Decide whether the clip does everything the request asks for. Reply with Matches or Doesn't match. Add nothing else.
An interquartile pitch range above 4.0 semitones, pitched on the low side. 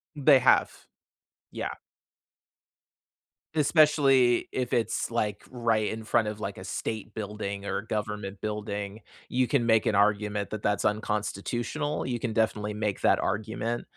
Doesn't match